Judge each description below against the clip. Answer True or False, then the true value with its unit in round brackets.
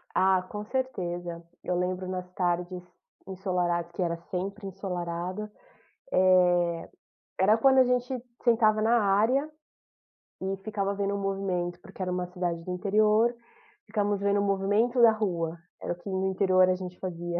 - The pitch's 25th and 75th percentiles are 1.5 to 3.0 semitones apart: True (2.7 semitones)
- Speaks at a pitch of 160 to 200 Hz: True (190 Hz)